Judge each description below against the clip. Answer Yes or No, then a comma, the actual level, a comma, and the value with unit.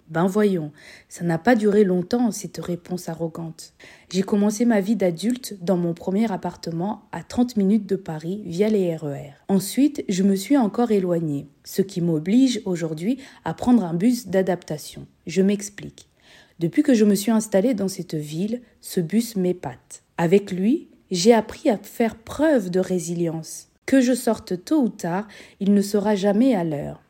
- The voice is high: Yes, high, 195 Hz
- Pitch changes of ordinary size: Yes, average, 4.7 semitones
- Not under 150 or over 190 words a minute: Yes, average, 170 wpm